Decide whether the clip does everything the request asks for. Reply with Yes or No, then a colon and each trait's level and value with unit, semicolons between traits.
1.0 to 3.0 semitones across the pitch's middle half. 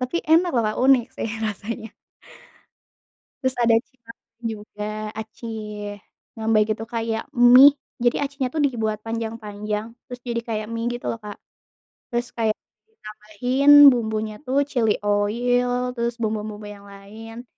Yes: narrow, 2.5 semitones